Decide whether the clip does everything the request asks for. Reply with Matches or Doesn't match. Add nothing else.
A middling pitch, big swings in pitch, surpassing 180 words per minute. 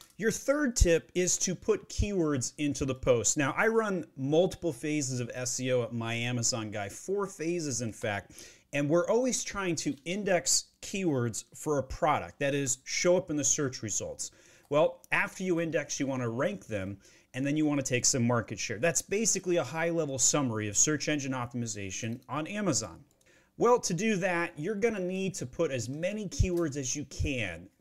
Matches